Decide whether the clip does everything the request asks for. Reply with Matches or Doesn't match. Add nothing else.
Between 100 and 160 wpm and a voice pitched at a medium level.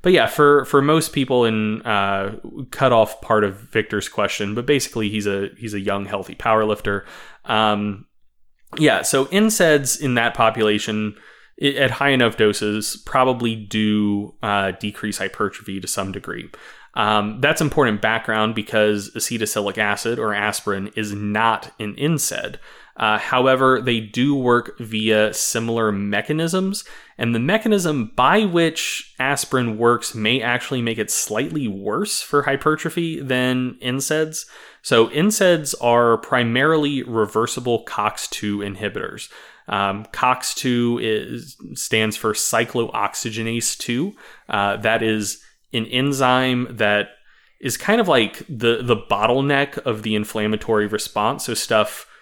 Doesn't match